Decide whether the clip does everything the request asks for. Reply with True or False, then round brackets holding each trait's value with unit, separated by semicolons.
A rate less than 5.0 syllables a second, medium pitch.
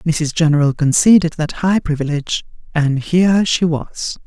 True (4.7 syllables/s; 160 Hz)